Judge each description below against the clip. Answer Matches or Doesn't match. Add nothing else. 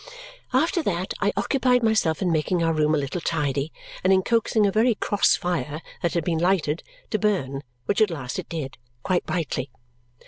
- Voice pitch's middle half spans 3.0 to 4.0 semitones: Doesn't match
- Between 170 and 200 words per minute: Matches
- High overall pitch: Doesn't match